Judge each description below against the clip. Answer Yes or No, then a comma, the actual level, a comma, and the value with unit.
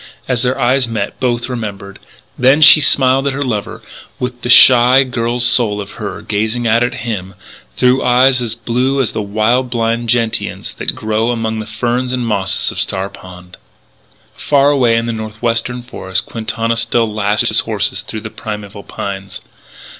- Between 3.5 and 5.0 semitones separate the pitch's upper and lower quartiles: No, average, 2.7 semitones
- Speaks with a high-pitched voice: No, low, 115 Hz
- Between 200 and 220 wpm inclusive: No, average, 170 wpm